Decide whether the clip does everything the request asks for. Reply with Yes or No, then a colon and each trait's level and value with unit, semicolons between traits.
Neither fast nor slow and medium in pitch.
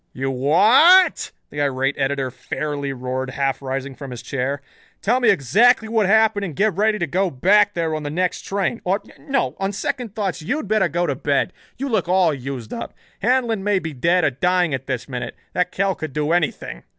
No: fast, 210 wpm; medium, 170 Hz